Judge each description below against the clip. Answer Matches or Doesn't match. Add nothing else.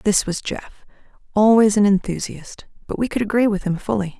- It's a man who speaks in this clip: Doesn't match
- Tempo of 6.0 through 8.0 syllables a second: Doesn't match